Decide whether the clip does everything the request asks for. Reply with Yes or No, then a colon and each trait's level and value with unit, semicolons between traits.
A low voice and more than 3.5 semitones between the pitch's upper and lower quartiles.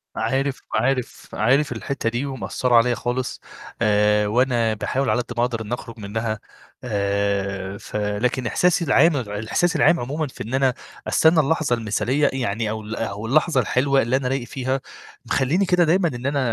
Yes: low, 125 Hz; average, 4.1 semitones